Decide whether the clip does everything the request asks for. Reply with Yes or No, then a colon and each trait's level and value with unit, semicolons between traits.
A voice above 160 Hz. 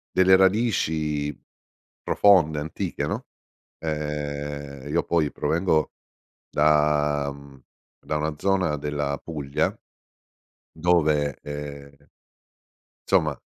No: very low, 75 Hz